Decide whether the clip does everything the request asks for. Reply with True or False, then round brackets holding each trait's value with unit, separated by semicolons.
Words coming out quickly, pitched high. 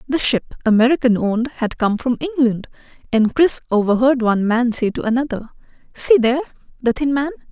False (170 wpm; 250 Hz)